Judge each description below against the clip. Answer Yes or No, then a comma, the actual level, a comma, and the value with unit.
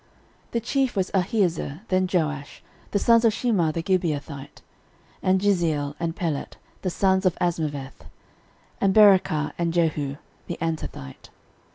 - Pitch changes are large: No, average, 4.0 semitones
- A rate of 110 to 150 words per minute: Yes, average, 140 wpm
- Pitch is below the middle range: No, medium, 175 Hz